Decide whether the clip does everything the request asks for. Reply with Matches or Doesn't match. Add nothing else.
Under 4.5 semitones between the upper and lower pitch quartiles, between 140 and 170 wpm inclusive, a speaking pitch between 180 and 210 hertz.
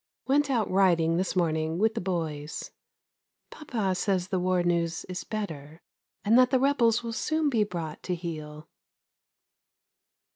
Doesn't match